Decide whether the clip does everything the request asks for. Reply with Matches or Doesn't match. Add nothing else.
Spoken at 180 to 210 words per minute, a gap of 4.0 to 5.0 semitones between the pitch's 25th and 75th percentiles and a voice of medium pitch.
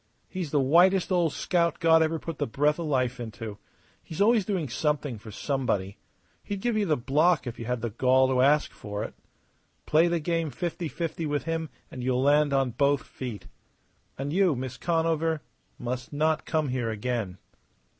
Matches